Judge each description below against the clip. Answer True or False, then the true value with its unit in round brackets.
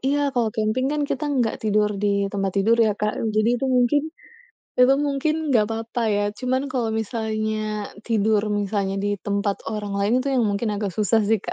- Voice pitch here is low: False (220 Hz)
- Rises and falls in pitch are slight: False (3.3 semitones)